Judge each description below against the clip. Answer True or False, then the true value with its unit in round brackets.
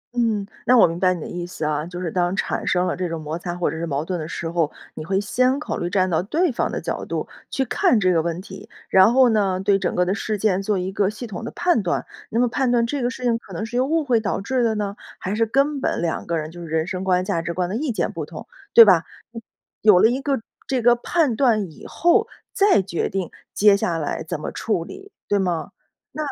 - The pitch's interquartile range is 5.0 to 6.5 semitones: True (5.4 semitones)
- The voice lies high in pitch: True (195 Hz)